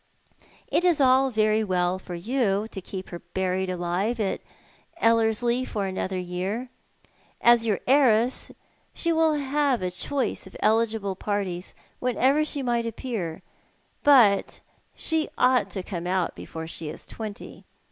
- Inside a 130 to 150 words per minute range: Yes, average, 145 wpm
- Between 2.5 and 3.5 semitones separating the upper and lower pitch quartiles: No, average, 5.3 semitones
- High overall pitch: Yes, high, 215 Hz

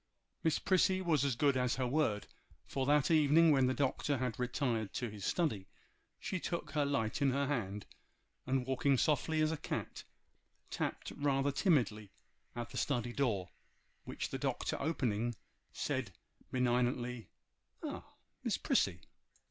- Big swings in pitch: No, average, 3.5 semitones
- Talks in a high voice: No, low, 130 Hz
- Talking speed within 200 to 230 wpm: No, average, 150 wpm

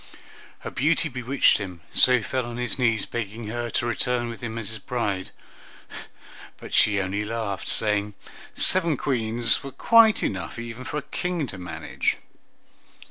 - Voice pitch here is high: No, low, 115 Hz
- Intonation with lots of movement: No, average, 3.4 semitones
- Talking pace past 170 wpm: No, average, 160 wpm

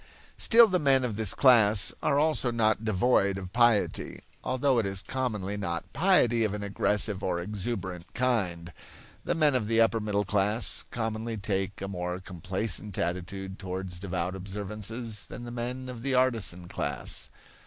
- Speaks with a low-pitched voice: Yes, low, 105 Hz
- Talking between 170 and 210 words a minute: No, average, 160 wpm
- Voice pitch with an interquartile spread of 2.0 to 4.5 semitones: Yes, average, 4.0 semitones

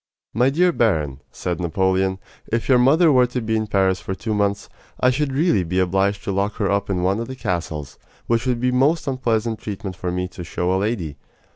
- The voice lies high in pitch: No, low, 105 Hz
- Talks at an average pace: No, fast, 220 wpm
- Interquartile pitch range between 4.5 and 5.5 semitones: Yes, average, 5.0 semitones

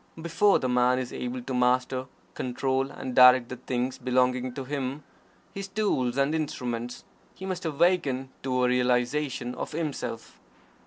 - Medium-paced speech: Yes, average, 150 wpm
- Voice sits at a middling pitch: No, low, 130 Hz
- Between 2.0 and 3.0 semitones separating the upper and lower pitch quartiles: Yes, average, 2.7 semitones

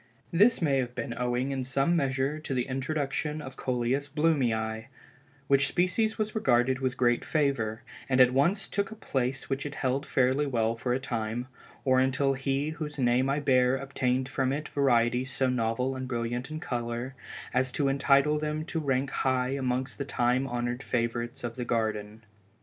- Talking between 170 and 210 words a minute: Yes, average, 180 wpm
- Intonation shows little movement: Yes, narrow, 2.3 semitones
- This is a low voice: Yes, low, 130 Hz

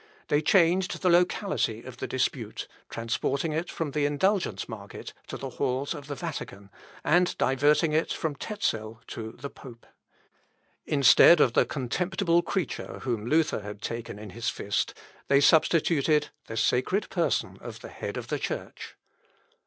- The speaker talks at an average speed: Yes, average, 155 wpm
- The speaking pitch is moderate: Yes, medium, 145 Hz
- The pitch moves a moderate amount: No, wide, 6.1 semitones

